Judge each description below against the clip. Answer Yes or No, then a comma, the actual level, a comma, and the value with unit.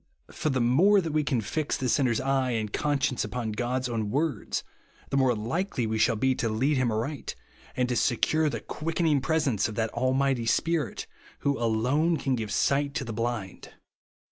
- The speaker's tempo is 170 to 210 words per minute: Yes, average, 190 wpm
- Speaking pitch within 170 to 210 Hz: No, low, 130 Hz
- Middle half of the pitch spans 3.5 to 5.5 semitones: Yes, average, 4.0 semitones